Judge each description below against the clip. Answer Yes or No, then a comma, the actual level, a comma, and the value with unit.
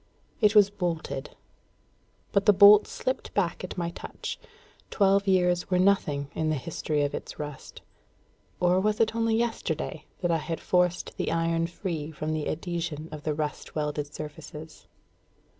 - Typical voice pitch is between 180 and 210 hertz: No, medium, 170 Hz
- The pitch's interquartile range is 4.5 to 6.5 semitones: No, average, 4.1 semitones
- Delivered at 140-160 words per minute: Yes, average, 155 wpm